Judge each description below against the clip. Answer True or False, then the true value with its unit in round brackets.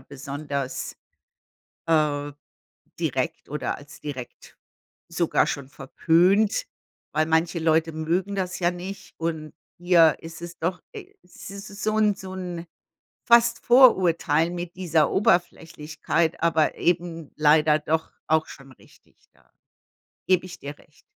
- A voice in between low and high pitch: True (165 Hz)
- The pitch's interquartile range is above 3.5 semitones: False (2.8 semitones)